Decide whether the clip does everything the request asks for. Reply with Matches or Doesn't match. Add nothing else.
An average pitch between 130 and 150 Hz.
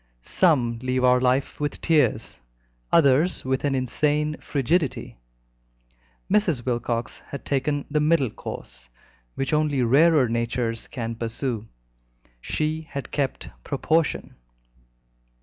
Matches